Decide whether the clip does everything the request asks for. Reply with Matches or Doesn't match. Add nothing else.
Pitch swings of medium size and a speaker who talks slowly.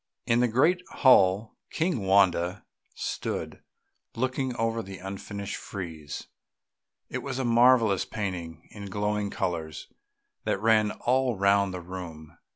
Matches